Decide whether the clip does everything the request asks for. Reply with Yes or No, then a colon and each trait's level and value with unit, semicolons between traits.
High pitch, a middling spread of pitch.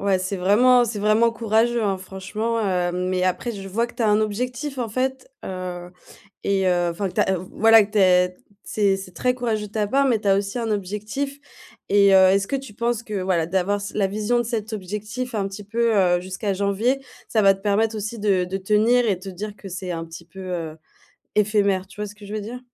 Yes: high, 205 Hz; average, 3.0 semitones